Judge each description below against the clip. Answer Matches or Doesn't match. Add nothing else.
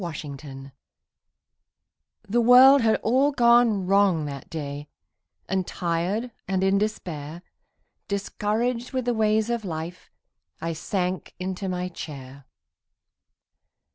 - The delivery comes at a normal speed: Doesn't match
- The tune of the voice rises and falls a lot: Matches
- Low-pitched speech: Doesn't match